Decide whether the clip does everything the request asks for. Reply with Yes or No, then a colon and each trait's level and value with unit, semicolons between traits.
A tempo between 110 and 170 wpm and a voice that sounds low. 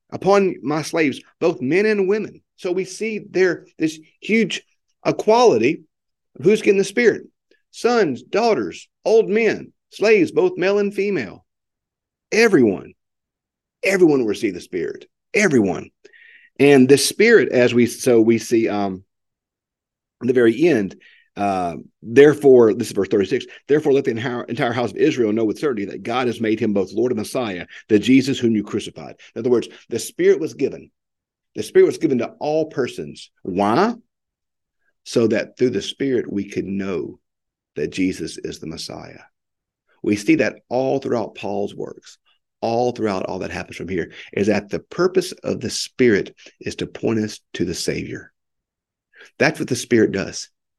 No: average, 165 wpm; medium, 150 Hz